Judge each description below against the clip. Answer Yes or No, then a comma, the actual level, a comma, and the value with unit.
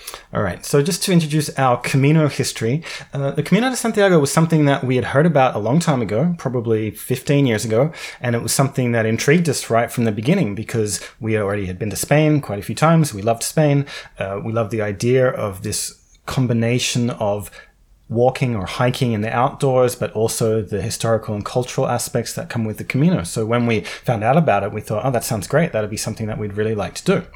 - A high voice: No, low, 120 Hz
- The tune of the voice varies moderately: Yes, average, 4.6 semitones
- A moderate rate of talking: No, fast, 225 wpm